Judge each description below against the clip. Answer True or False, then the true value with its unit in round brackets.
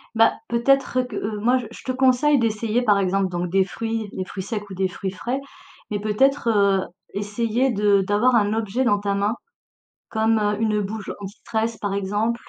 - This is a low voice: False (210 Hz)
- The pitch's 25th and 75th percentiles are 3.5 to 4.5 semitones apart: False (2.8 semitones)